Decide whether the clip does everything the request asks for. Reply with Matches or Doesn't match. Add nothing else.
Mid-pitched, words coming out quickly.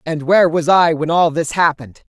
Matches